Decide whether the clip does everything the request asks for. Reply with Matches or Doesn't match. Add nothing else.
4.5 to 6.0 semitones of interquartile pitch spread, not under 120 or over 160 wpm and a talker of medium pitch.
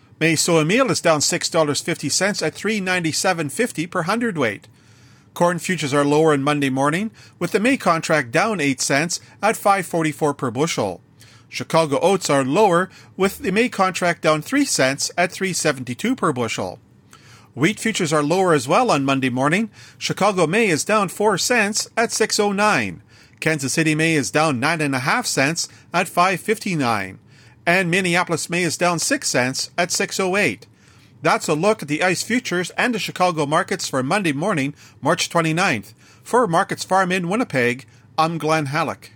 Matches